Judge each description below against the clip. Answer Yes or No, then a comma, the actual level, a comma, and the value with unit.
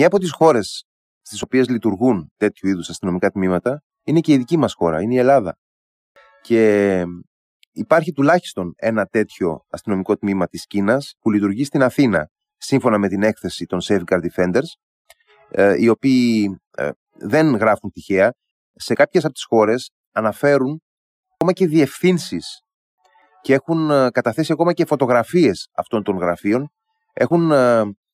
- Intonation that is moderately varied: No, wide, 7.3 semitones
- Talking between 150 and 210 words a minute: No, average, 135 wpm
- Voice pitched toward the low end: Yes, low, 120 Hz